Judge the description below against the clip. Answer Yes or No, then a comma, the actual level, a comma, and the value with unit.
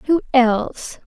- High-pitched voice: Yes, very high, 250 Hz